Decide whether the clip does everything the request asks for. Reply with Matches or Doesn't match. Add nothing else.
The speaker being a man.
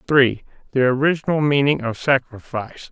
Matches